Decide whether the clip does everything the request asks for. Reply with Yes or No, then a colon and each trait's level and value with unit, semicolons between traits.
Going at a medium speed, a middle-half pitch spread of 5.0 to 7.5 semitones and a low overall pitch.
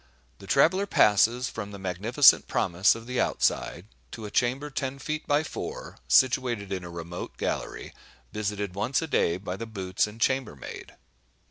Yes: average, 160 wpm; wide, 5.4 semitones; low, 110 Hz